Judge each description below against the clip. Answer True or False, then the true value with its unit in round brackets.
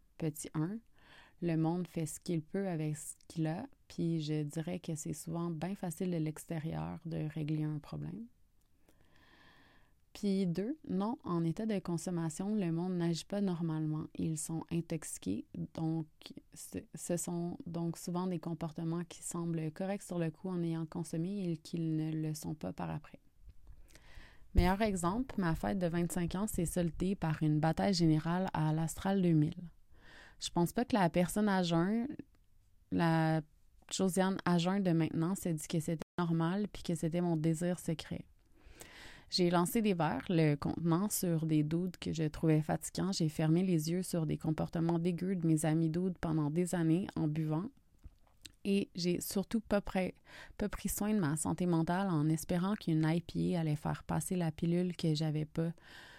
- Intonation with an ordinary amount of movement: False (2.3 semitones)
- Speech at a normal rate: True (170 wpm)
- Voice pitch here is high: False (170 Hz)